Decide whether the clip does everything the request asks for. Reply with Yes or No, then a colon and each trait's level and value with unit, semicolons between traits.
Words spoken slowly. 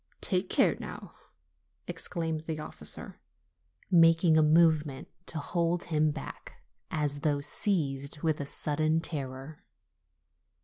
Yes: slow, 115 wpm